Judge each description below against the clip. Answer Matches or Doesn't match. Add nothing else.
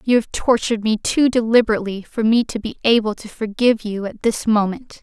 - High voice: Matches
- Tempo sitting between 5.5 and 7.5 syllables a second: Matches